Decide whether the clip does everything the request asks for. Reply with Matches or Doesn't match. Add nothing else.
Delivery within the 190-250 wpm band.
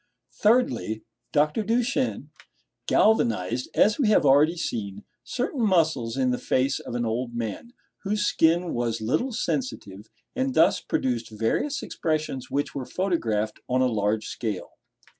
Doesn't match